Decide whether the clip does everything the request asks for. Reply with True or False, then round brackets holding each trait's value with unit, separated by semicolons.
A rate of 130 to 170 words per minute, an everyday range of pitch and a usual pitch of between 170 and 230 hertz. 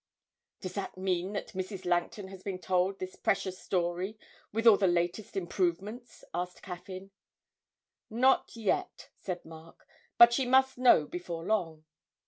True (140 wpm; 3.0 semitones; 185 Hz)